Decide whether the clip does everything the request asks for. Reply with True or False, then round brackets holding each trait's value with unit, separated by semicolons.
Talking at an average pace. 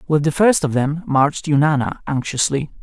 True (170 wpm)